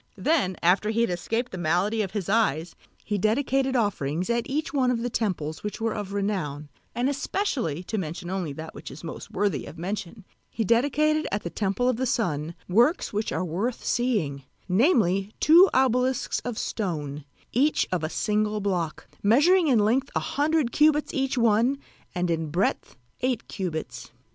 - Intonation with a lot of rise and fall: Yes, wide, 6.1 semitones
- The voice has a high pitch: Yes, high, 210 Hz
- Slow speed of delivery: No, average, 175 wpm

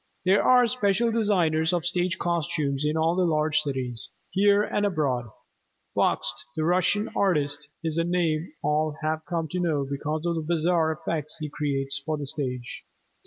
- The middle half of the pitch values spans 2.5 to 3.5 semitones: Yes, average, 3.2 semitones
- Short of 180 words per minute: Yes, average, 165 wpm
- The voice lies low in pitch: No, medium, 160 Hz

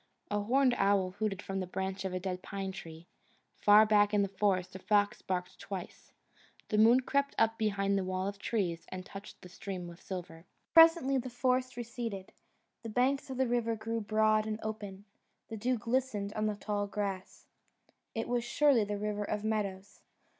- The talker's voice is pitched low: No, high, 210 Hz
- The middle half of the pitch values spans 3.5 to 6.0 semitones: No, average, 3.0 semitones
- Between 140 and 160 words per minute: No, average, 185 wpm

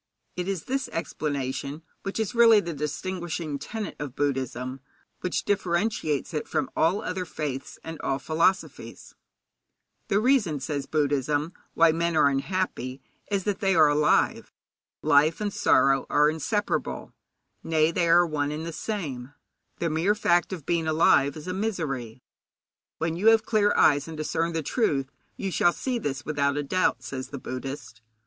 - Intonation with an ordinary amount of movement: Yes, average, 4.6 semitones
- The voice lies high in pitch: No, medium, 160 Hz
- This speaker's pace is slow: No, average, 160 wpm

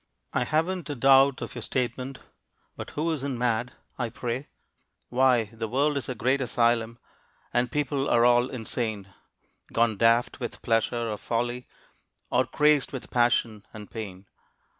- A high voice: No, low, 120 Hz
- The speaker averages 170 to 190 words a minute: No, average, 150 wpm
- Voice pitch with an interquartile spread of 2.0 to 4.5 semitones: Yes, narrow, 2.6 semitones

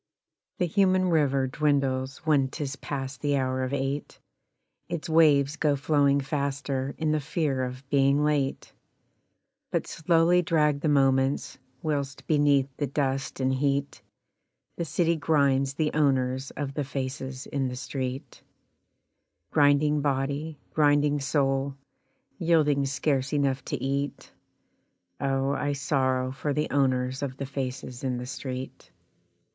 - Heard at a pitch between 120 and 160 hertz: Yes, medium, 140 Hz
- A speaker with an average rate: No, slow, 130 wpm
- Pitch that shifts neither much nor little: No, narrow, 1.9 semitones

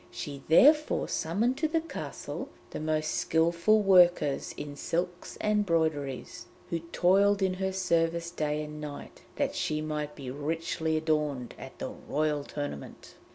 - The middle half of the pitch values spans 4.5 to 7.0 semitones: No, average, 3.7 semitones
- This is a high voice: No, medium, 160 Hz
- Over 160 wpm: No, average, 145 wpm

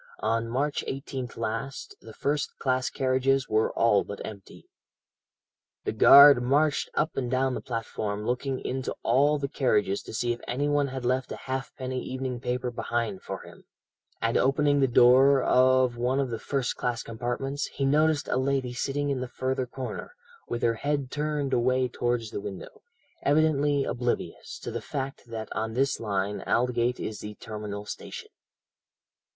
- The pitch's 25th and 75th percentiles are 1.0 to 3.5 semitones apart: Yes, average, 2.8 semitones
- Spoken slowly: No, average, 165 wpm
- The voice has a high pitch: No, low, 130 Hz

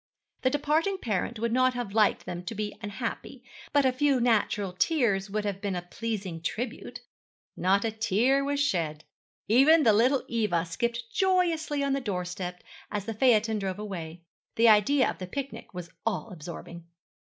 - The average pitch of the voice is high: Yes, high, 220 Hz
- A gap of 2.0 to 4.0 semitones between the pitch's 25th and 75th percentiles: No, average, 5.2 semitones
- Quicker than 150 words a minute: Yes, average, 170 wpm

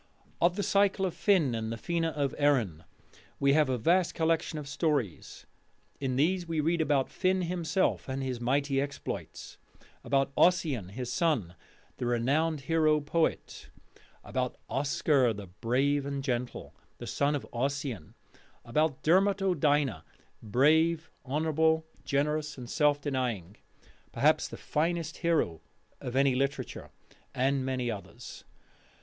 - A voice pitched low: No, medium, 145 Hz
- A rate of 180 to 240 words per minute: No, slow, 135 wpm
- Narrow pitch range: No, average, 4.1 semitones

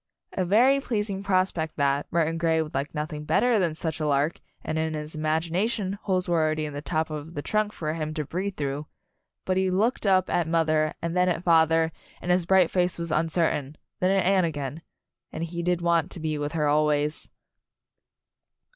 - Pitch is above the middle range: No, medium, 165 Hz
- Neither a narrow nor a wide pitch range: Yes, average, 3.1 semitones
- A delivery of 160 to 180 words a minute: No, average, 200 wpm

